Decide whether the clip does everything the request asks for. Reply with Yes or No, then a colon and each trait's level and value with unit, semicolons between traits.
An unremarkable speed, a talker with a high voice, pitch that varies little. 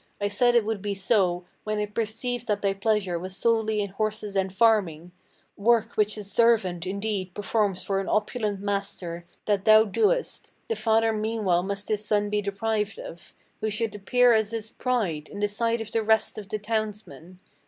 Yes: average, 185 wpm; high, 210 Hz; narrow, 2.1 semitones